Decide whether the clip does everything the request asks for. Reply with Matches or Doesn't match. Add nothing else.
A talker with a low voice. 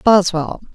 Doesn't match